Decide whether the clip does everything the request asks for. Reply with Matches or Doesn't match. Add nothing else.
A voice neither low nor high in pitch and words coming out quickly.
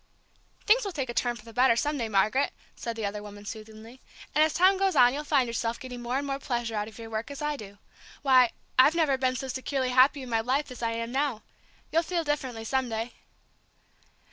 Doesn't match